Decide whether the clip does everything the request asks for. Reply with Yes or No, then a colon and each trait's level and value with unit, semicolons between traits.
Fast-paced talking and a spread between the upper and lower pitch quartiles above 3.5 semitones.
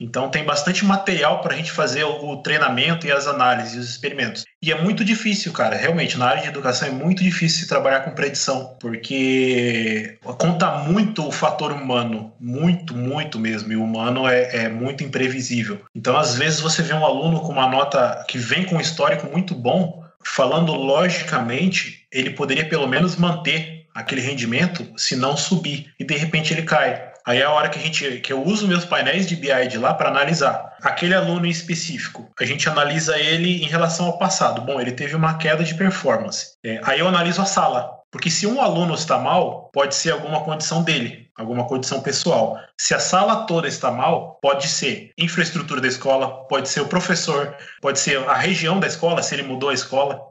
Yes: fast, 195 wpm; average, 4.5 semitones